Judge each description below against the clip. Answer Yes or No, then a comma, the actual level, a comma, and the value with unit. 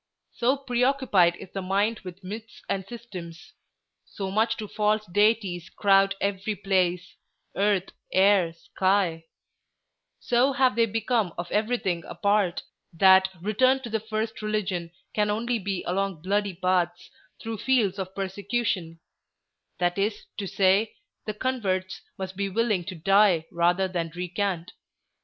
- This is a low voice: No, high, 195 Hz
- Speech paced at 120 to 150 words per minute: Yes, slow, 135 wpm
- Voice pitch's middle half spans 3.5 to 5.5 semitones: No, average, 2.9 semitones